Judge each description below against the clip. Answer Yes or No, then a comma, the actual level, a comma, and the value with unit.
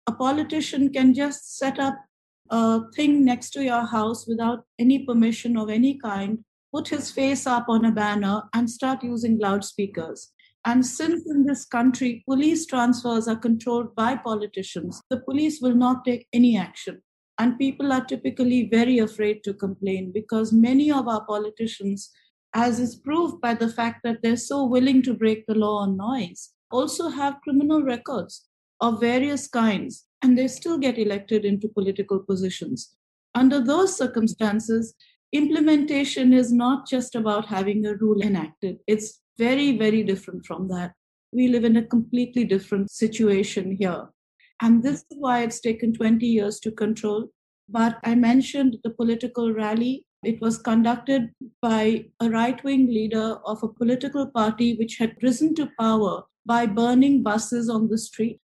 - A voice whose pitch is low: No, high, 235 Hz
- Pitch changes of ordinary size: Yes, average, 3.1 semitones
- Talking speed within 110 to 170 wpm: Yes, average, 160 wpm